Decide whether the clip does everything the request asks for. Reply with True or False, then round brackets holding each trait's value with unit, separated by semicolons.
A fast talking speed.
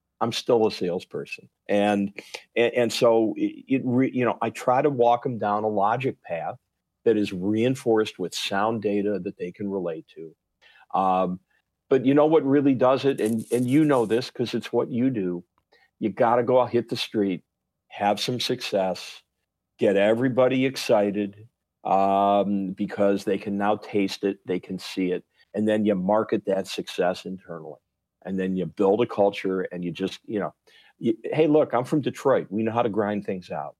False (190 wpm)